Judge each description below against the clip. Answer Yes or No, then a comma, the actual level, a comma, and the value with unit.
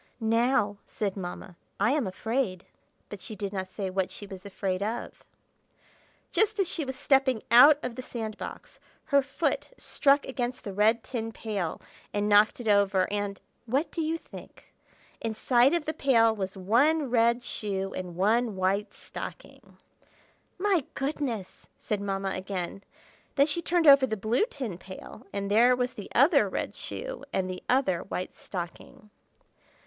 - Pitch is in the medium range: No, high, 220 Hz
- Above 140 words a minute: Yes, average, 160 wpm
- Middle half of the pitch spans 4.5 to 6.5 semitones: Yes, average, 5.3 semitones